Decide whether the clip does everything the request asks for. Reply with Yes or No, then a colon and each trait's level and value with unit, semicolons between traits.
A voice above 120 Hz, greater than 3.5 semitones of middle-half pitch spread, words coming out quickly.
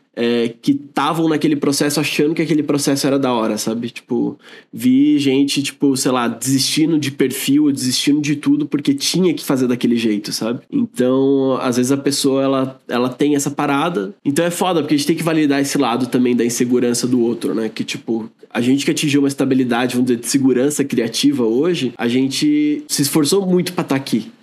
Yes: medium, 140 Hz; average, 4.0 semitones; fast, 200 wpm